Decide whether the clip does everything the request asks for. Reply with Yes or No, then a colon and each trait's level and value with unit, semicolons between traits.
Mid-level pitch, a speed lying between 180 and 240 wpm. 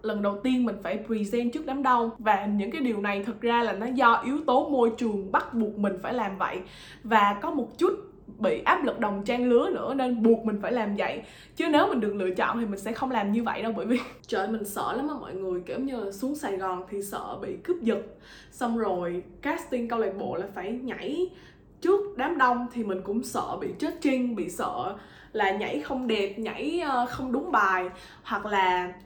No: high, 230 Hz; average, 230 wpm